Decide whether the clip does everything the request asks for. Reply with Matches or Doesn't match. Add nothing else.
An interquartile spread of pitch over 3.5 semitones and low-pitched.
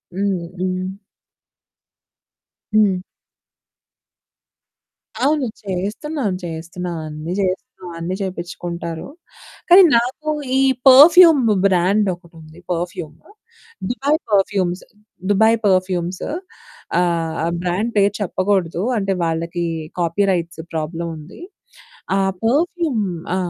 Doesn't match